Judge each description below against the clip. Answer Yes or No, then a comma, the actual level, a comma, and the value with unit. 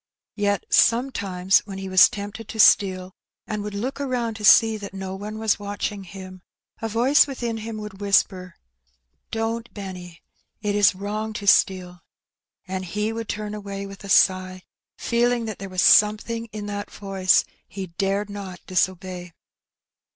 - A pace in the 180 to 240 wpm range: No, average, 160 wpm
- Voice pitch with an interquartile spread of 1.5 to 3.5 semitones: Yes, narrow, 2.6 semitones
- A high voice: Yes, high, 205 Hz